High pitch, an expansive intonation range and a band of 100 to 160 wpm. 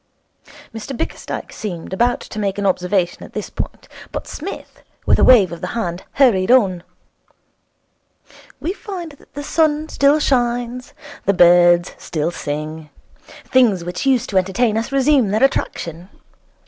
Yes: high, 215 Hz; wide, 6.9 semitones; average, 150 wpm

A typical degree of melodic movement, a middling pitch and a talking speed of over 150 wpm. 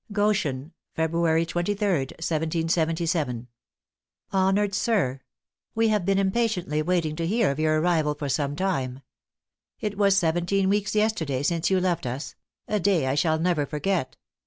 No: average, 4.3 semitones; medium, 170 Hz; average, 140 wpm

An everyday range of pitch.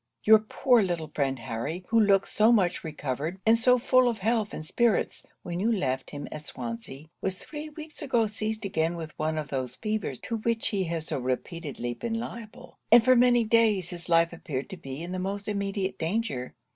No: wide, 6.5 semitones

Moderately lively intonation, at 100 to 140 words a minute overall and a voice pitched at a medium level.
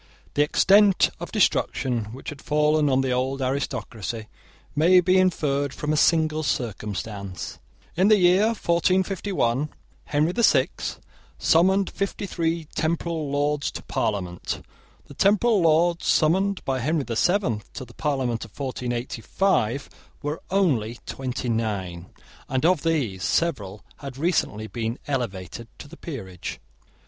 No: wide, 6.3 semitones; slow, 135 wpm; medium, 145 Hz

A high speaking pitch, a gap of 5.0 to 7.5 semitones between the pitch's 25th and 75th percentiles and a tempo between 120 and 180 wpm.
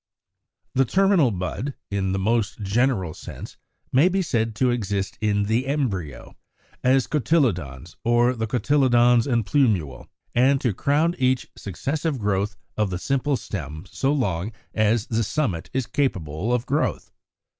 No: low, 120 Hz; average, 5.3 semitones; average, 145 wpm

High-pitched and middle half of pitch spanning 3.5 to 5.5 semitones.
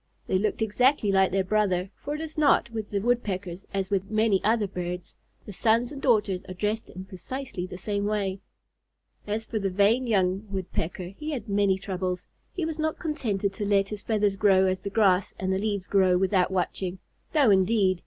No: high, 200 Hz; average, 2.7 semitones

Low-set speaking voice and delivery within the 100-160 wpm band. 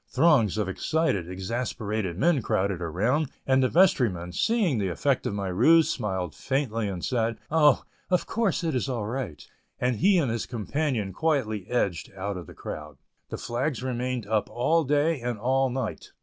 No: low, 120 Hz; average, 175 wpm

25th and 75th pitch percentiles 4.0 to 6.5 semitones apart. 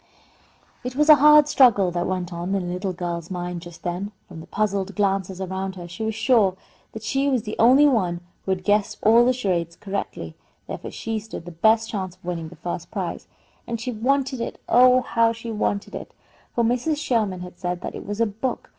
Yes: average, 4.6 semitones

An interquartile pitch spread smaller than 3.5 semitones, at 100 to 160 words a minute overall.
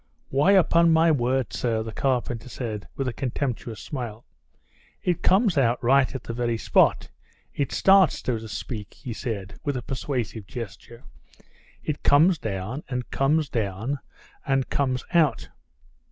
No: average, 3.9 semitones; average, 150 wpm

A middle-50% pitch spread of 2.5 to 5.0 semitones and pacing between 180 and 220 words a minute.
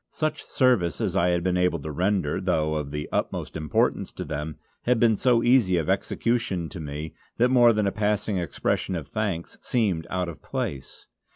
No: wide, 5.5 semitones; average, 190 wpm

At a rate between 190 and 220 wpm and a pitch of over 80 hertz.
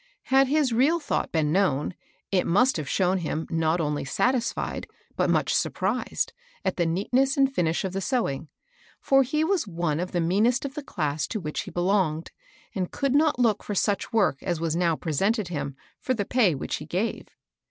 Yes: average, 195 wpm; high, 190 Hz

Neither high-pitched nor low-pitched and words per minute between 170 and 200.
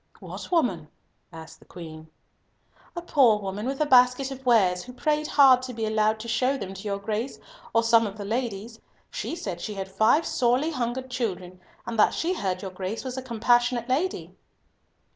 No: high, 230 Hz; average, 190 wpm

